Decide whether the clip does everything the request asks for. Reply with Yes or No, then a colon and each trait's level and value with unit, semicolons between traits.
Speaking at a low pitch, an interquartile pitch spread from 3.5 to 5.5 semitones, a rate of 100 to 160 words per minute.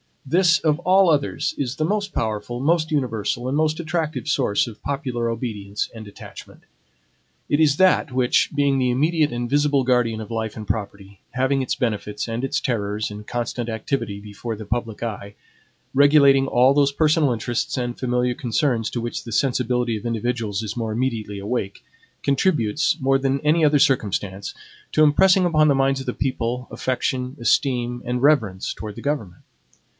No: low, 125 Hz; average, 4.1 semitones; average, 170 wpm